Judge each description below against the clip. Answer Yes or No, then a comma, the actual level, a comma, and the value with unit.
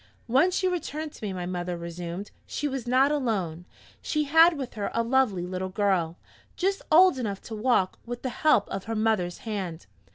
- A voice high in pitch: Yes, high, 225 Hz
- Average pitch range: No, wide, 6.9 semitones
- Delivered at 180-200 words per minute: Yes, average, 190 wpm